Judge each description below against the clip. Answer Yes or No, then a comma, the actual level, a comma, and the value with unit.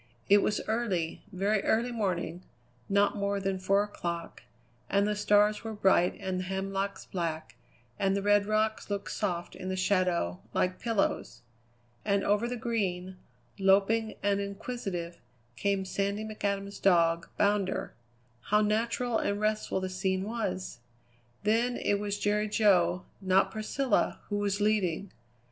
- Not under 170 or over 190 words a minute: No, average, 140 wpm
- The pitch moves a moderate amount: No, narrow, 2.1 semitones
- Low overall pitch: No, high, 200 Hz